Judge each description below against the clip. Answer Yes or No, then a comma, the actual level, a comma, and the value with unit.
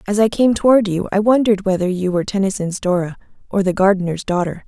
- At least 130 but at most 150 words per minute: No, fast, 205 wpm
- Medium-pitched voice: No, high, 195 Hz